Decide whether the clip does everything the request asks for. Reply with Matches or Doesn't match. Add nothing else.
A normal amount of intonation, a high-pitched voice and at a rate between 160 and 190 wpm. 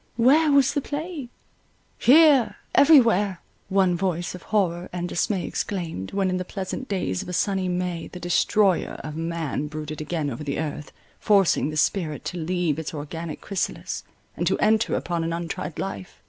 Doesn't match